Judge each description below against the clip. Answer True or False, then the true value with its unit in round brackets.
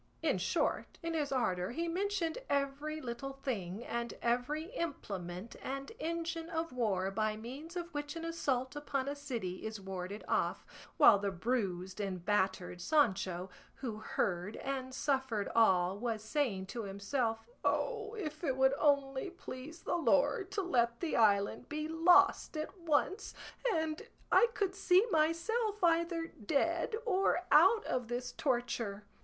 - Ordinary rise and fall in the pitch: False (7.3 semitones)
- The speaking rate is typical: True (150 wpm)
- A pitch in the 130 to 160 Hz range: False (270 Hz)